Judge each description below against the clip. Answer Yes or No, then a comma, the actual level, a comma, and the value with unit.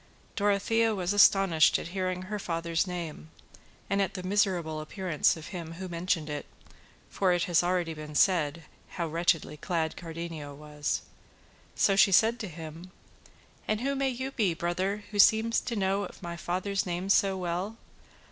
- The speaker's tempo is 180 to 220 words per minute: No, average, 160 wpm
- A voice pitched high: No, medium, 180 Hz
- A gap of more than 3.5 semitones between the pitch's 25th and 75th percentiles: No, average, 3.1 semitones